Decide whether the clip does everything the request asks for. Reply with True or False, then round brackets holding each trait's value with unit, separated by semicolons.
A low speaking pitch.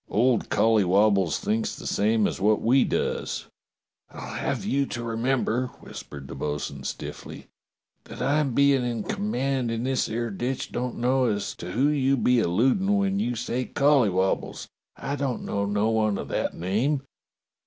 True (120 Hz)